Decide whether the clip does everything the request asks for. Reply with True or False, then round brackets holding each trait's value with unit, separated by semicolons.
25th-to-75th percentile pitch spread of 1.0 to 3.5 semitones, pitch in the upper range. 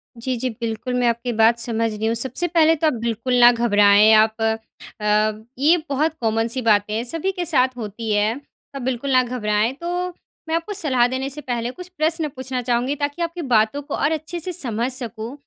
False (4.3 semitones; 245 Hz)